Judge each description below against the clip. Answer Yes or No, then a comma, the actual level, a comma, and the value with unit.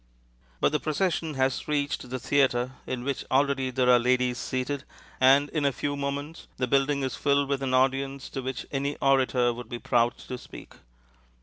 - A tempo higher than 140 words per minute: Yes, average, 185 wpm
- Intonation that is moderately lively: No, narrow, 1.9 semitones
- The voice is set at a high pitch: No, low, 135 Hz